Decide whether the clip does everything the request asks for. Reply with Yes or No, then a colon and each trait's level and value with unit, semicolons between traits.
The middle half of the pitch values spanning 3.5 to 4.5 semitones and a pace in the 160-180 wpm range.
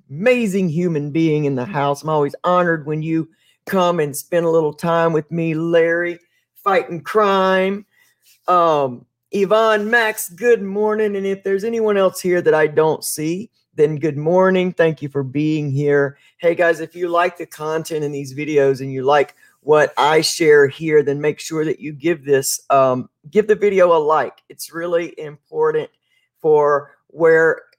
Yes: average, 4.0 semitones; average, 175 wpm